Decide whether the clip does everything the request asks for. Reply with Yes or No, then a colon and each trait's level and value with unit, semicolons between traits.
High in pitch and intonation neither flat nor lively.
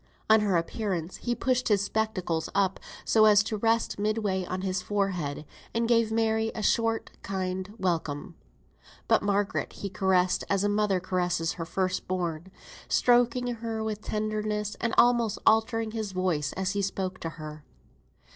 Yes: high, 200 Hz; average, 3.1 semitones